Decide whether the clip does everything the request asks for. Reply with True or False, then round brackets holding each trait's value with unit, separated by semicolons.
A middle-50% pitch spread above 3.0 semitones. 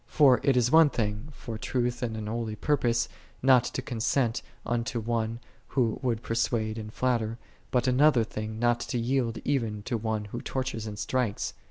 False (2.4 semitones)